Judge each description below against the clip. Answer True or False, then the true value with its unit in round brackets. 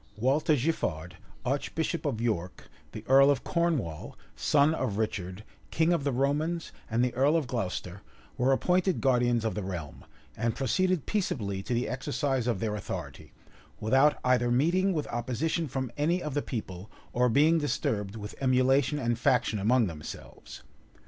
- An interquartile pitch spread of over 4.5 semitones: True (5.2 semitones)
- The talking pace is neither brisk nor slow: True (155 wpm)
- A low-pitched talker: True (125 Hz)